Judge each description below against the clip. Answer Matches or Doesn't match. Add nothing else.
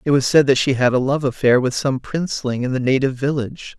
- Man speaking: Matches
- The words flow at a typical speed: Doesn't match